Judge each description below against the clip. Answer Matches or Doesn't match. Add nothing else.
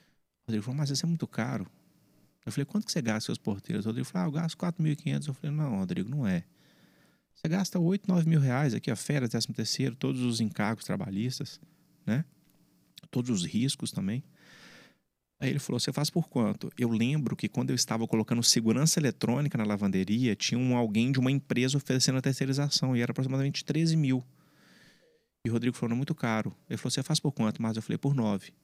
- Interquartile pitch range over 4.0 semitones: Matches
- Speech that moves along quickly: Matches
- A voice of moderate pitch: Doesn't match